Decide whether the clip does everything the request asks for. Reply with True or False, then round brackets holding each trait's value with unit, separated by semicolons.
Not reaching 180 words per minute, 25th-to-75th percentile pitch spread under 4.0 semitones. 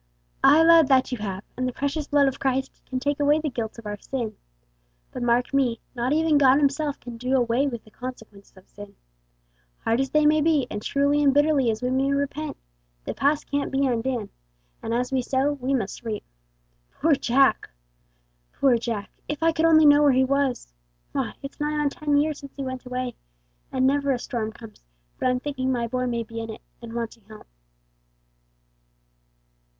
False (195 wpm; 3.4 semitones)